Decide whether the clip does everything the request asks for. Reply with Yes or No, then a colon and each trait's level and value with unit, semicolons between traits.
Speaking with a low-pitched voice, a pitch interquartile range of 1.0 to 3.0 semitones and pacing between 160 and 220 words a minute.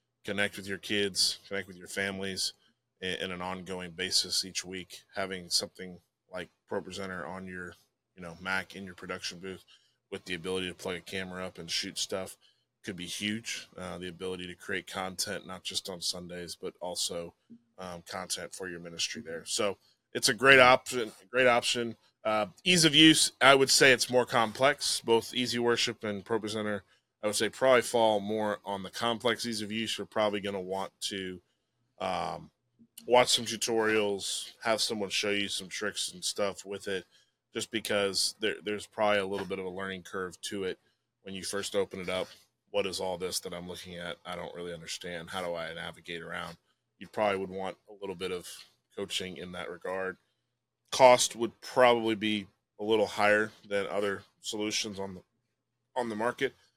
No: low, 100 Hz; average, 3.8 semitones; average, 190 wpm